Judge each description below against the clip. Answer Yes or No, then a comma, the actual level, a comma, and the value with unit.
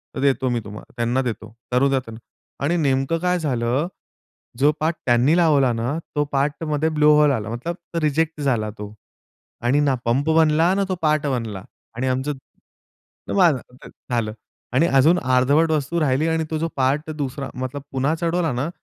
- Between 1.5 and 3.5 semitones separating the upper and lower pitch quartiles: No, average, 3.9 semitones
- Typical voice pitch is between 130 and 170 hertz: Yes, medium, 140 Hz